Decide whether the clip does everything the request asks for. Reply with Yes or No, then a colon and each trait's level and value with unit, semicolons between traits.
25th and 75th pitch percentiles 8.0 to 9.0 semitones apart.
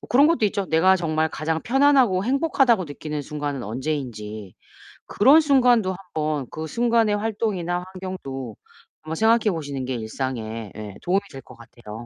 Yes: wide, 8.7 semitones